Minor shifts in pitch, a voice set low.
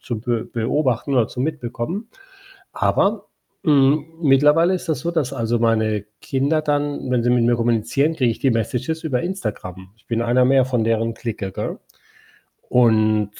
No: average, 4.3 semitones; low, 125 Hz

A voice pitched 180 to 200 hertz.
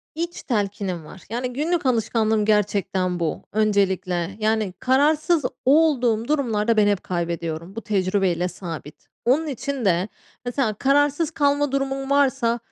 No: high, 225 Hz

